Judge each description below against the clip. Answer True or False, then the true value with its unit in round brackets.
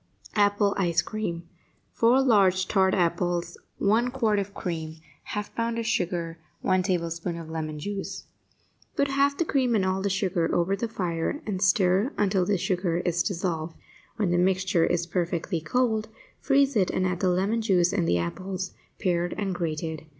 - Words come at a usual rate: True (170 wpm)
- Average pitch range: True (3.3 semitones)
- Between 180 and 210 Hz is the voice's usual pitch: True (185 Hz)